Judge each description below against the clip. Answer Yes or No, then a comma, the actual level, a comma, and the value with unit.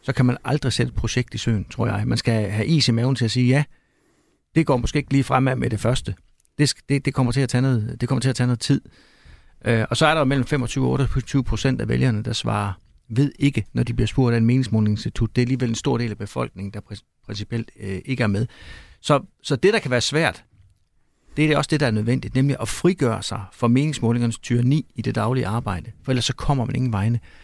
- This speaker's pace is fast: Yes, fast, 255 wpm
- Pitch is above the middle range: No, low, 120 Hz